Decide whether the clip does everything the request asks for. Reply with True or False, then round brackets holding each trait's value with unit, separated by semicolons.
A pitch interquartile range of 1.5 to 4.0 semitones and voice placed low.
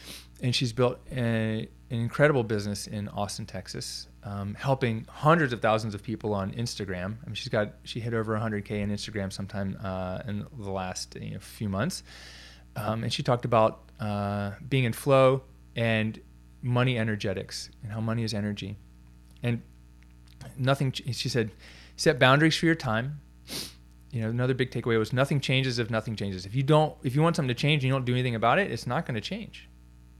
False (4.7 semitones; 110 Hz)